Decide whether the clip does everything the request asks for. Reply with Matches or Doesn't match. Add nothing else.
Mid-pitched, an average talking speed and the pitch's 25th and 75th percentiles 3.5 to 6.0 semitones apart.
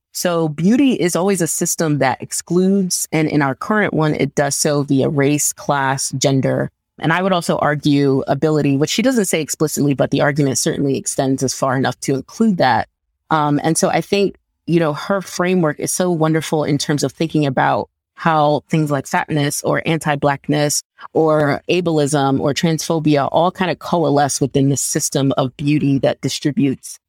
Doesn't match